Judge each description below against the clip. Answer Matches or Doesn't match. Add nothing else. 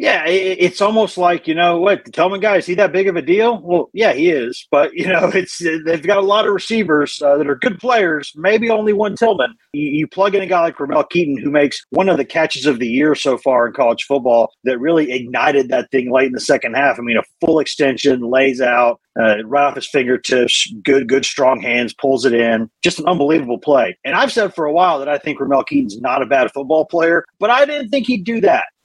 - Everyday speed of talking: Doesn't match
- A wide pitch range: Matches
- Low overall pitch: Doesn't match